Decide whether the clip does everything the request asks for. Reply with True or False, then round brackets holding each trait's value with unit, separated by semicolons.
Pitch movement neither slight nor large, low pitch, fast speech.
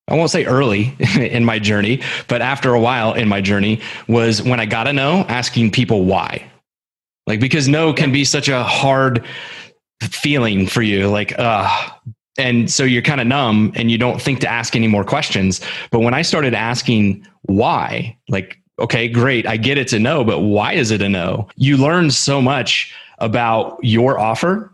False (3.5 semitones; 120 Hz; 190 wpm)